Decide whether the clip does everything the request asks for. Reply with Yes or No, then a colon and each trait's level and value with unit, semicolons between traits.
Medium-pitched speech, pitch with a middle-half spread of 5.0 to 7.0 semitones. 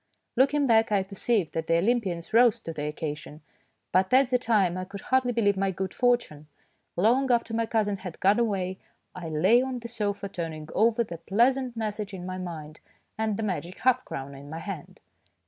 No: high, 200 Hz; wide, 5.4 semitones